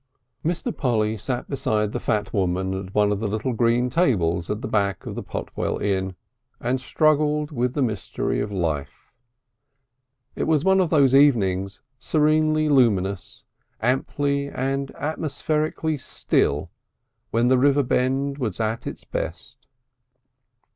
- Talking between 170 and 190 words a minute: No, average, 140 wpm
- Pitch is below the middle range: Yes, low, 125 Hz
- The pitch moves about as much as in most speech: No, wide, 5.8 semitones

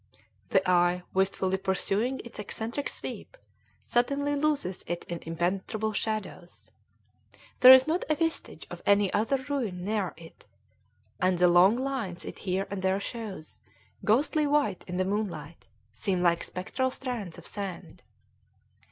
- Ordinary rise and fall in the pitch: No, wide, 5.8 semitones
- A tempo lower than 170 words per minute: Yes, average, 140 wpm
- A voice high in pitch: Yes, high, 200 Hz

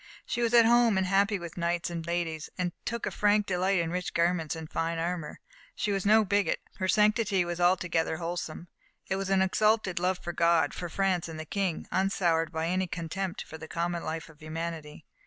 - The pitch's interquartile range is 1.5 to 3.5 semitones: Yes, average, 2.8 semitones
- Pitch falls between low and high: Yes, medium, 175 Hz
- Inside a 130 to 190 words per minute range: No, fast, 205 wpm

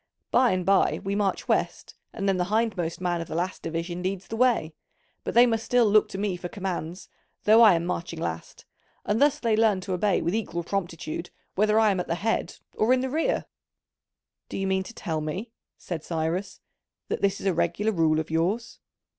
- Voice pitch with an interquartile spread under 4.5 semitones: Yes, average, 4.1 semitones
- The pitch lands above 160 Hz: Yes, high, 190 Hz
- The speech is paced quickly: Yes, fast, 210 wpm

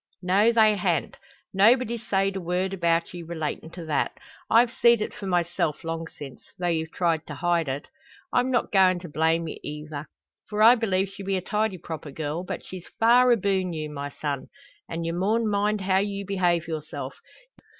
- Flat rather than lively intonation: No, average, 3.8 semitones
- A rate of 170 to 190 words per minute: Yes, average, 185 wpm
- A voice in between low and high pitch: Yes, medium, 180 Hz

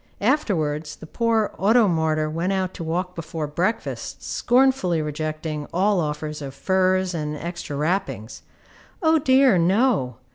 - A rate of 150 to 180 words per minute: No, slow, 135 wpm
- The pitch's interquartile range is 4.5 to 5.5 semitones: Yes, average, 4.9 semitones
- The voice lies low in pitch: No, medium, 175 Hz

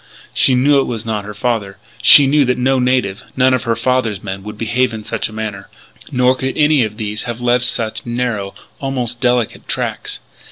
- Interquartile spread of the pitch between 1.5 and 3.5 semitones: Yes, average, 3.0 semitones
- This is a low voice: Yes, low, 120 Hz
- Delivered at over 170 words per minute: Yes, average, 200 wpm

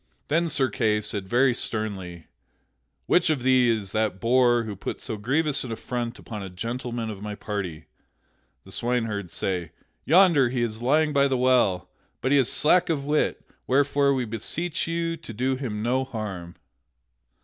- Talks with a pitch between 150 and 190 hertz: No, low, 120 Hz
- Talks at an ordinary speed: Yes, average, 170 wpm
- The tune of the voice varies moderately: Yes, average, 4.6 semitones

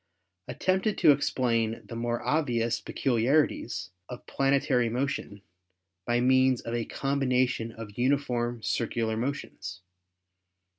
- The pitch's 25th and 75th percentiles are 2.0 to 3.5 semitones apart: Yes, average, 3.0 semitones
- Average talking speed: No, slow, 120 wpm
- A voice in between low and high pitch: No, low, 120 Hz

